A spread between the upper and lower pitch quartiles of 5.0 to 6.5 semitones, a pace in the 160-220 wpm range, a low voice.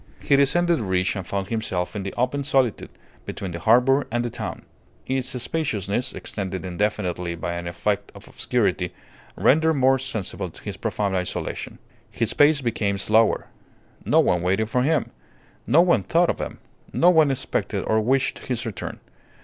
Yes: wide, 5.5 semitones; average, 165 wpm; low, 115 Hz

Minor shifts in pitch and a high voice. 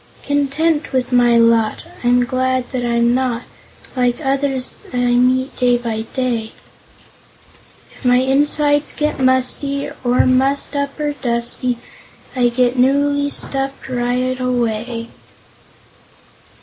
Yes: narrow, 2.1 semitones; very high, 255 Hz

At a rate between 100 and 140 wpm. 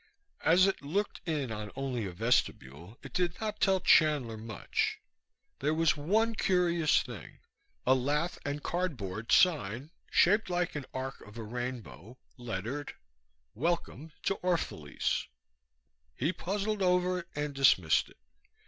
Yes: slow, 135 wpm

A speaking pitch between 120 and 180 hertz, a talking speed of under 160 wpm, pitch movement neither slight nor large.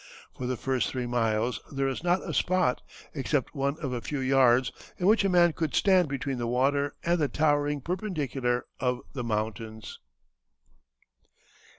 No: low, 135 Hz; average, 165 wpm; average, 4.0 semitones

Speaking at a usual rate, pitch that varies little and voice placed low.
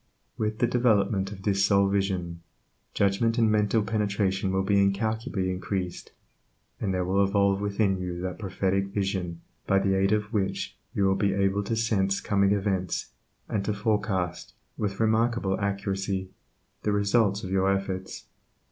Yes: average, 155 wpm; narrow, 1.5 semitones; low, 100 Hz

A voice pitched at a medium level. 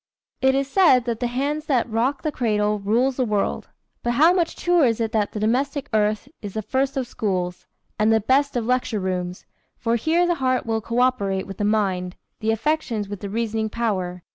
No: high, 230 Hz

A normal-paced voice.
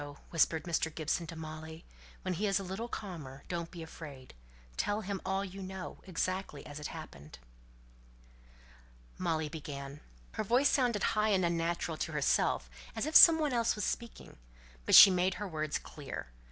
Yes: average, 165 wpm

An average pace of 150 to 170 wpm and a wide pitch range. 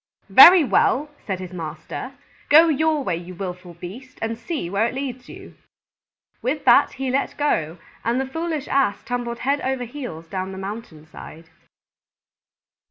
Yes: average, 160 wpm; wide, 7.1 semitones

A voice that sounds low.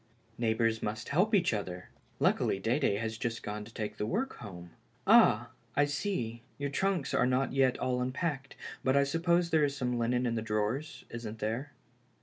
Yes: low, 125 Hz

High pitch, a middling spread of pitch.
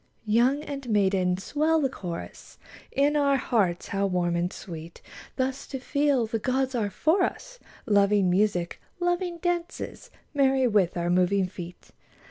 No: high, 225 Hz; wide, 7.3 semitones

